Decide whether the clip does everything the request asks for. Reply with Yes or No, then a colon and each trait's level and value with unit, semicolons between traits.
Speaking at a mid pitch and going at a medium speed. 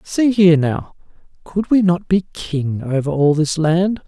Yes: medium, 170 Hz; average, 175 wpm